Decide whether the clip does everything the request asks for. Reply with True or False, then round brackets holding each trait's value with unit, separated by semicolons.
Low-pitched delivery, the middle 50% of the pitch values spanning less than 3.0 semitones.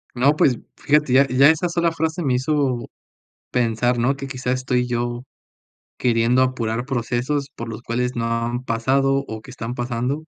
True (125 Hz; 2.5 semitones)